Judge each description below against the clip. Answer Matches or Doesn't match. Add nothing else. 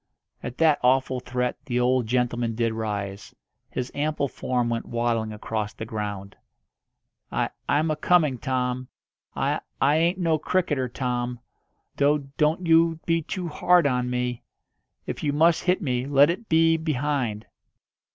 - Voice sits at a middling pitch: Doesn't match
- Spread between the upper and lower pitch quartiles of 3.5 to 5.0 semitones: Matches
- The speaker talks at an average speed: Matches